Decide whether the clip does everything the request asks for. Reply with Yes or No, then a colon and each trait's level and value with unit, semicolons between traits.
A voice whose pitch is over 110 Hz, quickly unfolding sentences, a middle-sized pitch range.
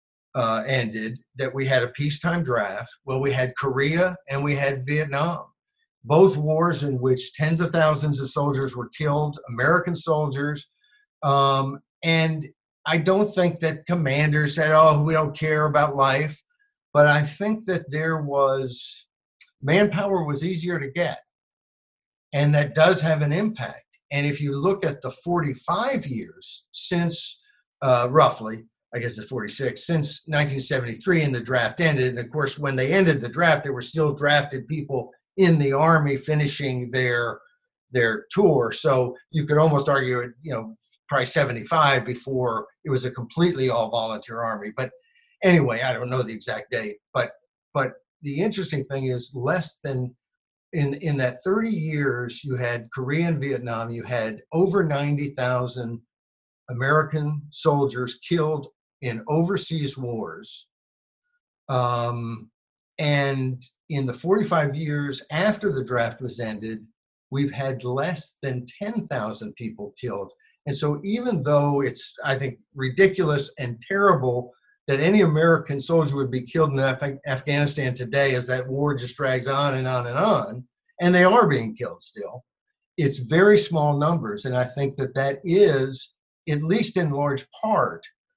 No: medium, 140 Hz; average, 150 wpm; average, 4.3 semitones